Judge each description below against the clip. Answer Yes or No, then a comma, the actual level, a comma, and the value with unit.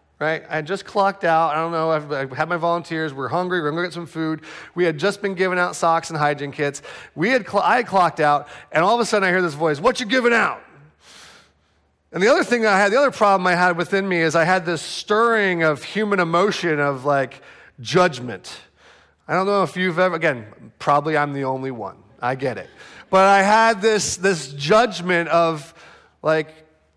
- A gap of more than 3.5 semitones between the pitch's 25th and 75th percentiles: Yes, average, 4.0 semitones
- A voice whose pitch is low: No, medium, 170 Hz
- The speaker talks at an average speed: No, fast, 220 wpm